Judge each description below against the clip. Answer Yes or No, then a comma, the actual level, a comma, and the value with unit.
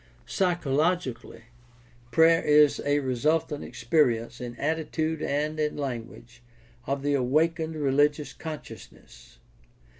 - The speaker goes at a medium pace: No, slow, 100 wpm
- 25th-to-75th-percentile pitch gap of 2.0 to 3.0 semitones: No, average, 3.6 semitones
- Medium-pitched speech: Yes, medium, 145 Hz